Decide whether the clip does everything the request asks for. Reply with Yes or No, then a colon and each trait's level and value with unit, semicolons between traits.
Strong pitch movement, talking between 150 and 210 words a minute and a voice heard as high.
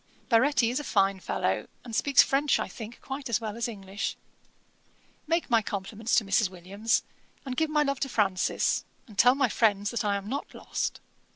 No: average, 4.8 semitones; average, 190 wpm; high, 230 Hz